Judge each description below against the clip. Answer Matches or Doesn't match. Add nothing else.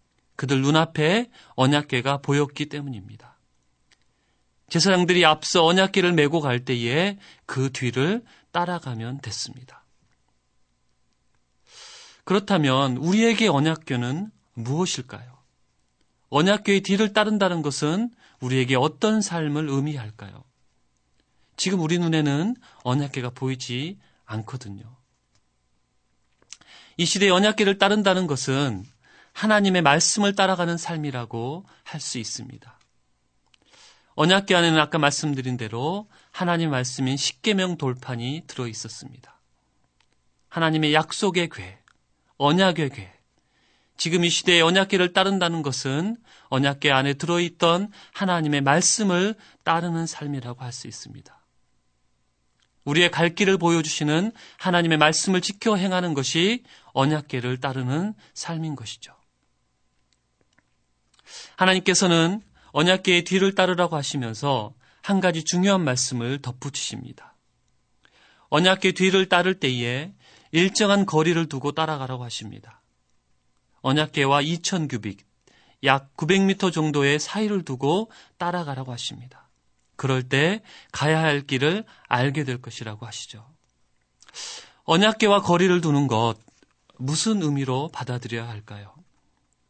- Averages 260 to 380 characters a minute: Matches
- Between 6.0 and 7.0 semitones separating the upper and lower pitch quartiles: Matches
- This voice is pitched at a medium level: Matches